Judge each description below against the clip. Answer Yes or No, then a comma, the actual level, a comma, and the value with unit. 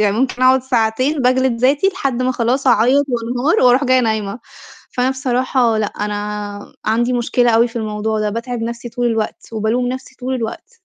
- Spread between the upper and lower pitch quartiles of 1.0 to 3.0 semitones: Yes, narrow, 2.6 semitones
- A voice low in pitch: No, high, 245 Hz